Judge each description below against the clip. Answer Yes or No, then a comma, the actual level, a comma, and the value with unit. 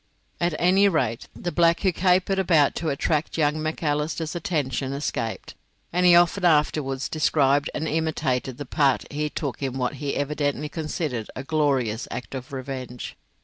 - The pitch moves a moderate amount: Yes, average, 3.4 semitones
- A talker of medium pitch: Yes, medium, 150 Hz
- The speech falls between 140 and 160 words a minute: Yes, average, 155 wpm